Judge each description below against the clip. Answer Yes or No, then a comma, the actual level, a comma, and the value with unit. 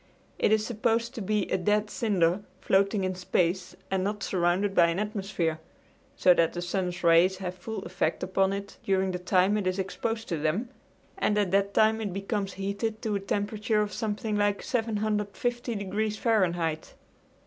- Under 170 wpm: No, average, 175 wpm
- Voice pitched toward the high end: Yes, high, 200 Hz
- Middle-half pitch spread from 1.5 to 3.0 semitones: Yes, narrow, 2.5 semitones